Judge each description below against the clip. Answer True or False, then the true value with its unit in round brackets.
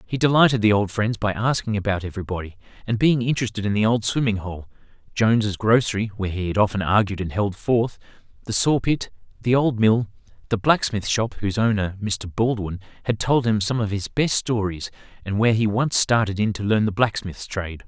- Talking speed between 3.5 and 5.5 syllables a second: False (5.7 syllables/s)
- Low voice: True (110 Hz)